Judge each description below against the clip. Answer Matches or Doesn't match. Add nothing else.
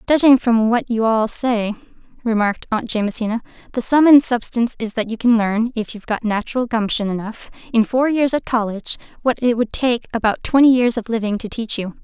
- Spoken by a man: Doesn't match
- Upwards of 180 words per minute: Matches